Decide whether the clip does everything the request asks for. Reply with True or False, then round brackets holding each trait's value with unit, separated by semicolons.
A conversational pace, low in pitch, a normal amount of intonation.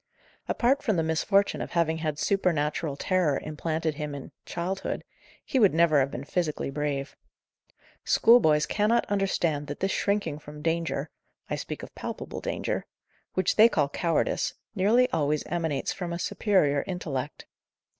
False (150 wpm; 165 Hz; 4.4 semitones)